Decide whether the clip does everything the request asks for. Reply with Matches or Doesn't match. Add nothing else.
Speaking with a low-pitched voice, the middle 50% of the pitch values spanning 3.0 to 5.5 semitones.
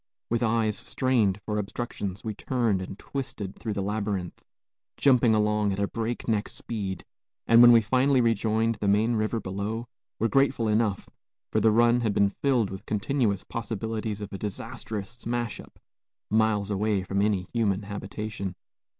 Doesn't match